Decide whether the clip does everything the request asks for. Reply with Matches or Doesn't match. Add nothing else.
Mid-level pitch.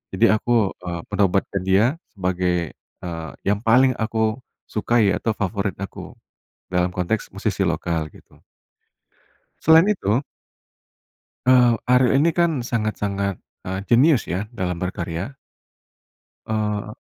Doesn't match